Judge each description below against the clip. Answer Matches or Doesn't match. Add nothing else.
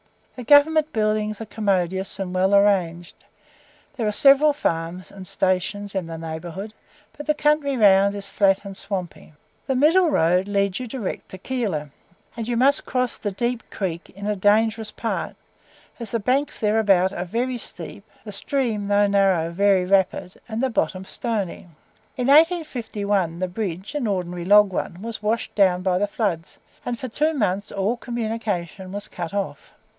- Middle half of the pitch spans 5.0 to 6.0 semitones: Doesn't match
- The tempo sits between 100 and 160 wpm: Doesn't match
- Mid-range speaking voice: Doesn't match